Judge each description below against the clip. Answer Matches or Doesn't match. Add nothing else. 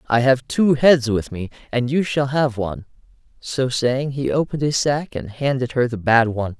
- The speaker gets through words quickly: Matches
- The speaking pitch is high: Doesn't match